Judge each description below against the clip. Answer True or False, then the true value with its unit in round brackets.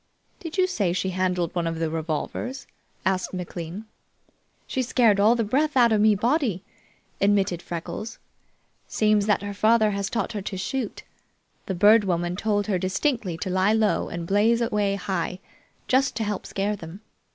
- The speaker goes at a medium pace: True (170 wpm)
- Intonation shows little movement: False (3.5 semitones)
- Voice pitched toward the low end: False (205 Hz)